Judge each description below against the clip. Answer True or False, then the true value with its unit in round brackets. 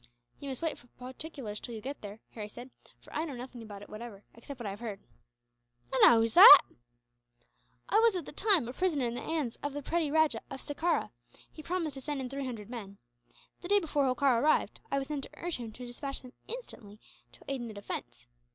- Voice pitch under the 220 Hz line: False (265 Hz)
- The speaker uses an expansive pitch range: False (5.0 semitones)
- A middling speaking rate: False (230 wpm)